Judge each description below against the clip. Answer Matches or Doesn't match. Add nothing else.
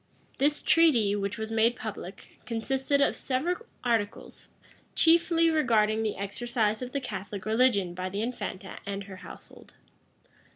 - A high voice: Matches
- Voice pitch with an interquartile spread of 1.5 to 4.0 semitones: Doesn't match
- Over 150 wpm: Doesn't match